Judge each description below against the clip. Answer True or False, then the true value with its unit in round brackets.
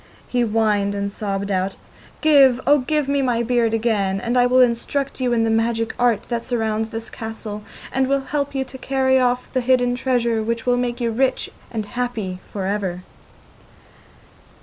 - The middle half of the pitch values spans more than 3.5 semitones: False (2.7 semitones)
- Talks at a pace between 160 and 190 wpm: True (185 wpm)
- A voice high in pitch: True (235 Hz)